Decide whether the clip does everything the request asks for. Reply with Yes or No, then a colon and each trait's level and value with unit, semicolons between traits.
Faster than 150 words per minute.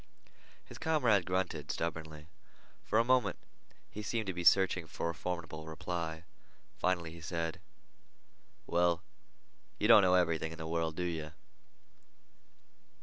No: slow, 135 wpm